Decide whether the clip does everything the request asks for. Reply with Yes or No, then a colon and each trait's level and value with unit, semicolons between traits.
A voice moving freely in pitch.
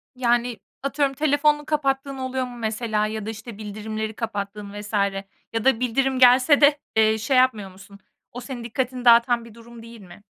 No: average, 3.3 semitones